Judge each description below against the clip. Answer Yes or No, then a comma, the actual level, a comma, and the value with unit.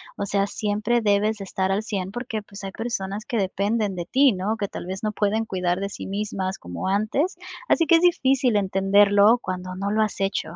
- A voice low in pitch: No, high, 205 Hz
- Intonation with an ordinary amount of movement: No, narrow, 2.2 semitones